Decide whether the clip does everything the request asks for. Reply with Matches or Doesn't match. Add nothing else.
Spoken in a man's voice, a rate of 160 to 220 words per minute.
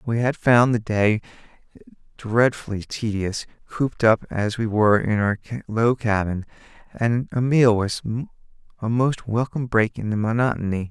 Doesn't match